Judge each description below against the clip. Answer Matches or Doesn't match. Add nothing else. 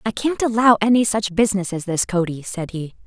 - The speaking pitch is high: Matches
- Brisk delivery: Matches